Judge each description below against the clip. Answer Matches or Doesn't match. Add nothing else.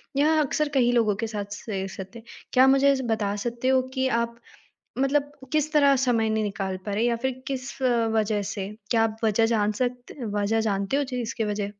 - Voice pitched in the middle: Doesn't match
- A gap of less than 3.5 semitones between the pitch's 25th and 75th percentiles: Doesn't match